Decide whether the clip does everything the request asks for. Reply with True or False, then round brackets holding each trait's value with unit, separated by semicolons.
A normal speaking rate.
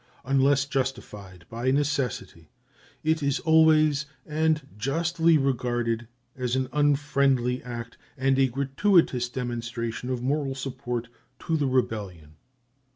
False (110 wpm)